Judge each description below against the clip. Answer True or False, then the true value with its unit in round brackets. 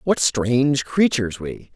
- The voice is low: True (125 Hz)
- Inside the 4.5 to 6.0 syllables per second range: False (4.2 syllables/s)